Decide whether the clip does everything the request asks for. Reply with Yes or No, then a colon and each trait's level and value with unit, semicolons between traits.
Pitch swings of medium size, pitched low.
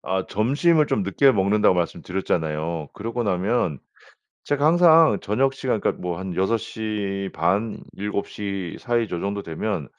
Yes: average, 4.1 semitones; low, 100 Hz